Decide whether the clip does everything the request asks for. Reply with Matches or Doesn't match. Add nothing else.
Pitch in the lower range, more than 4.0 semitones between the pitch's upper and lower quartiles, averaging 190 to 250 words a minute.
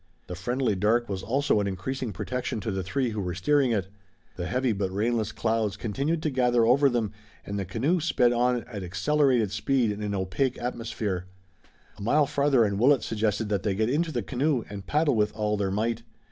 Matches